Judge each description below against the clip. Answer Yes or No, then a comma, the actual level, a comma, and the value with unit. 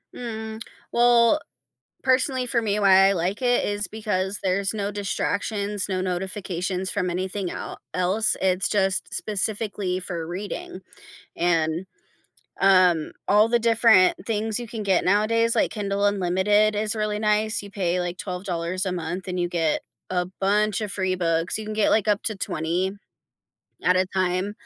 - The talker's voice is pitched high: Yes, high, 195 Hz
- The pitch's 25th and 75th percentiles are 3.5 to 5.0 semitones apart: No, narrow, 2.6 semitones